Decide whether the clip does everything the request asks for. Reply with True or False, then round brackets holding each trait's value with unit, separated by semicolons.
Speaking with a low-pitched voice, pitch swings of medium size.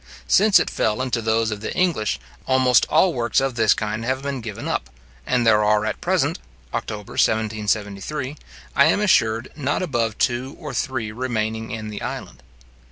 True (115 Hz; 3.4 semitones)